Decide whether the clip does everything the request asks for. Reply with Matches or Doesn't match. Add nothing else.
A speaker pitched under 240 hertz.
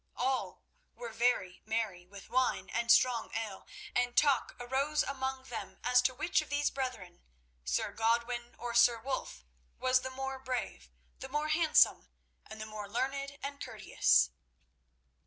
Doesn't match